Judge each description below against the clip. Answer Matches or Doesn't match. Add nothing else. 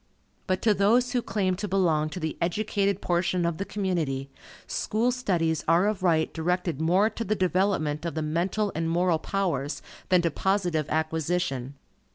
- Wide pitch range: Doesn't match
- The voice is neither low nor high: Matches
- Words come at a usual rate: Matches